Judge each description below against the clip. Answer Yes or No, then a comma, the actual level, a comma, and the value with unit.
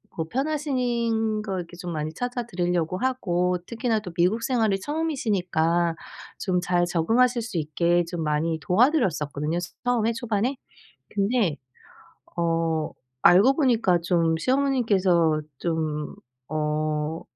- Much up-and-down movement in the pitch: Yes, wide, 6.2 semitones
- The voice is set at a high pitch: No, medium, 180 Hz